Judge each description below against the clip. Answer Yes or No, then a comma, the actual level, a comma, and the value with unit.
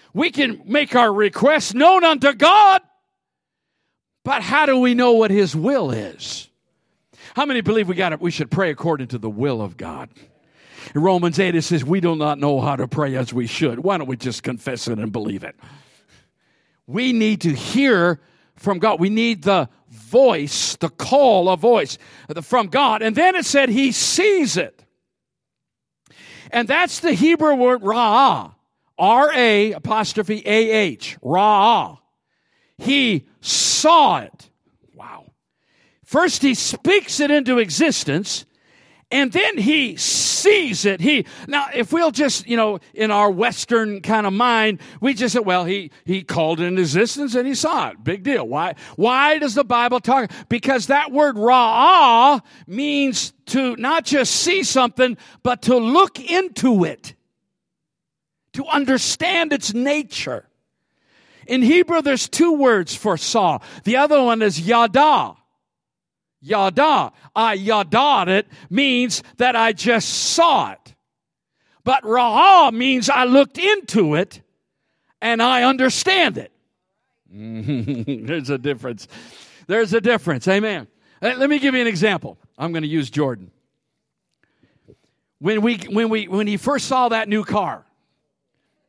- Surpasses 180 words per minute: No, average, 150 wpm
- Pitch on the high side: Yes, high, 230 Hz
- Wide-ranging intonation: Yes, wide, 7.7 semitones